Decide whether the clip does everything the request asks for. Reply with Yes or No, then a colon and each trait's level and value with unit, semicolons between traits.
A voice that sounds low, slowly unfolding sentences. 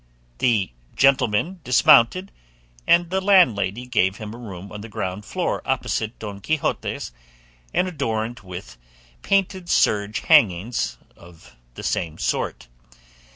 Yes: low, 110 Hz; slow, 120 wpm